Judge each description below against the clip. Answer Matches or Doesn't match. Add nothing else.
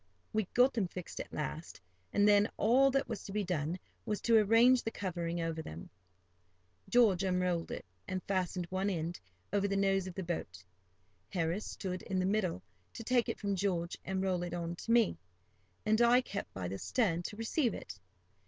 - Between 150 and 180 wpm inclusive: Doesn't match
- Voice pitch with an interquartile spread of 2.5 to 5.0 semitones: Matches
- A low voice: Doesn't match